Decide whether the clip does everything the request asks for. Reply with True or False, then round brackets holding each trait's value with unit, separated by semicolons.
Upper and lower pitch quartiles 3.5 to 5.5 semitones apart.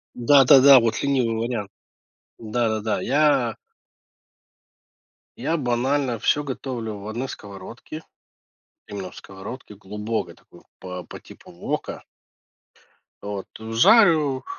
True (4.2 semitones)